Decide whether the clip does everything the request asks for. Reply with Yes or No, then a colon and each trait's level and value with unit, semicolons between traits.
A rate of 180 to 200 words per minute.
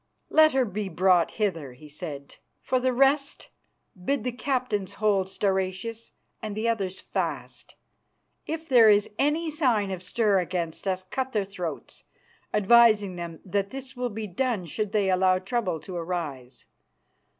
No: average, 150 wpm